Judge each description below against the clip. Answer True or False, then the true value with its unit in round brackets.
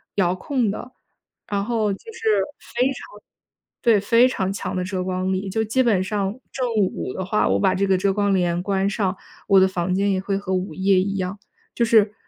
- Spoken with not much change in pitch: True (2.2 semitones)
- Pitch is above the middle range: True (195 Hz)